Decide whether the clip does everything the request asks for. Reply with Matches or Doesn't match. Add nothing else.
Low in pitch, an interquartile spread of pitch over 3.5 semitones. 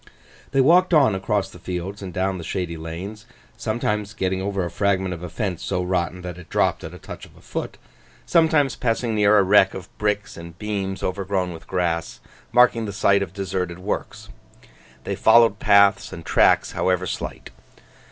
Doesn't match